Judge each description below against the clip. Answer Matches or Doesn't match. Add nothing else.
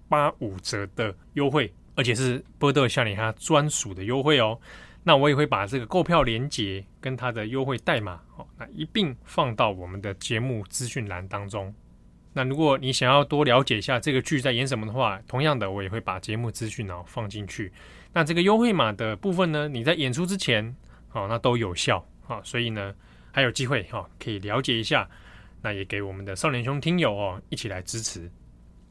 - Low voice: Matches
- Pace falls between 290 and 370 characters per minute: Matches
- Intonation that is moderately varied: Doesn't match